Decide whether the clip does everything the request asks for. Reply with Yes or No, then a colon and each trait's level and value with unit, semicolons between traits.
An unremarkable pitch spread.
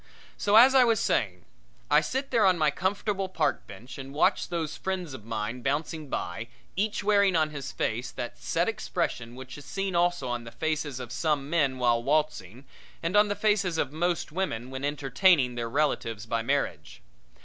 No: wide, 7.0 semitones